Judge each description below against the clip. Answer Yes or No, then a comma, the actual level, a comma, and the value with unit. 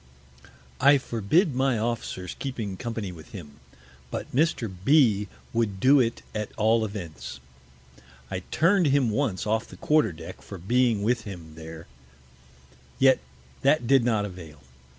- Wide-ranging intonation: Yes, wide, 5.8 semitones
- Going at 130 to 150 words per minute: Yes, average, 145 wpm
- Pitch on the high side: No, low, 110 Hz